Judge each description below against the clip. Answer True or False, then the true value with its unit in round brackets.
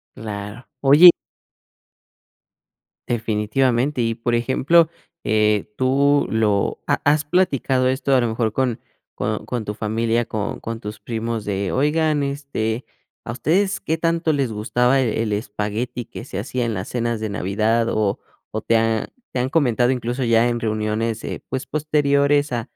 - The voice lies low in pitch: True (120 Hz)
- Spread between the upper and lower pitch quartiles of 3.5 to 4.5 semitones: True (3.9 semitones)